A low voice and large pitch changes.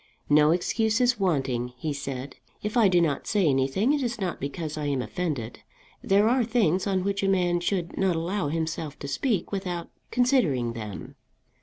No: medium, 175 Hz; wide, 6.1 semitones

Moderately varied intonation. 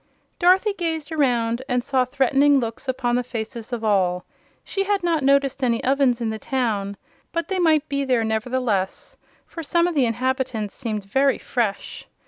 Yes: average, 4.0 semitones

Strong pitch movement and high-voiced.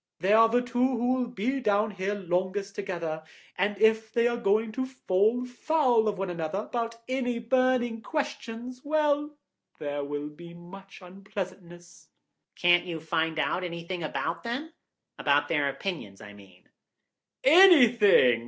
Yes: wide, 6.0 semitones; high, 205 Hz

